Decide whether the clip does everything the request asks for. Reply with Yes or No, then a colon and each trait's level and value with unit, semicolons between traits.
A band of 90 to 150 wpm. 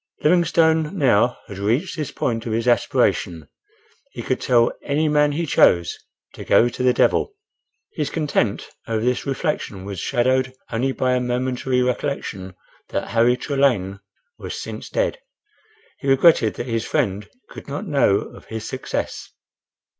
Yes: average, 145 wpm